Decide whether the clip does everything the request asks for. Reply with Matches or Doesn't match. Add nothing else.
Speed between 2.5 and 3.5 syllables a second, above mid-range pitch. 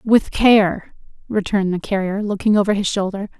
Doesn't match